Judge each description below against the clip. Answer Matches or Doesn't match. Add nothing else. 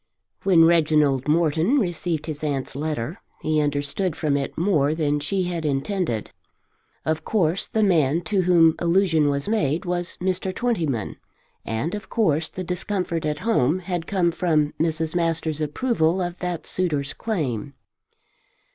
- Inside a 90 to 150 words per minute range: Matches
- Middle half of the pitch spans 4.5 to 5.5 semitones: Doesn't match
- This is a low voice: Doesn't match